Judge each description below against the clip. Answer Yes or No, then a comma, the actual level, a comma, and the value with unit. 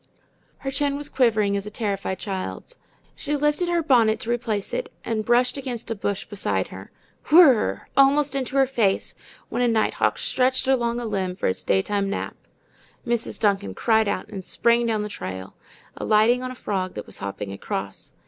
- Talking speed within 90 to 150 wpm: No, average, 180 wpm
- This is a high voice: Yes, high, 225 Hz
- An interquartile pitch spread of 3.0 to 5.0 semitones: Yes, average, 4.6 semitones